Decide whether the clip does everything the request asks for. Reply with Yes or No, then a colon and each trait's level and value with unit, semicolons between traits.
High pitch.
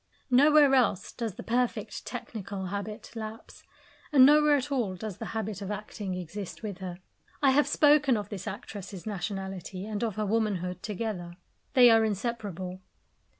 Yes: high, 210 Hz